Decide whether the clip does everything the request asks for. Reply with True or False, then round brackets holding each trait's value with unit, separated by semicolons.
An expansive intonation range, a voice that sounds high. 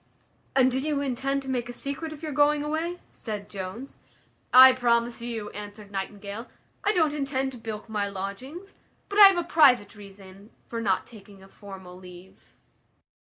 True (5.7 semitones; 240 Hz)